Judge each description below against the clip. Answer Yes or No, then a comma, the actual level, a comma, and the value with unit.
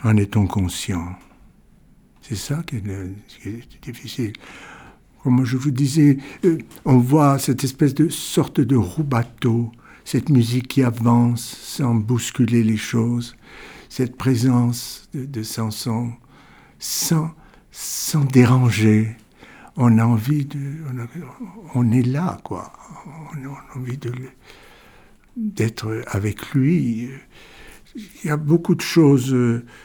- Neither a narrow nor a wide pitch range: Yes, average, 3.9 semitones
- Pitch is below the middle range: Yes, low, 125 Hz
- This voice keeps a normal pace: No, slow, 125 wpm